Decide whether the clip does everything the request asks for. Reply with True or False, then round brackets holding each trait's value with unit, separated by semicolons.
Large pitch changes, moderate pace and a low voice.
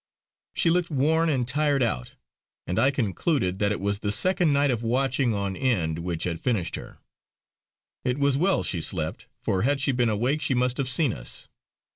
True (6.0 semitones; 190 wpm; 125 Hz)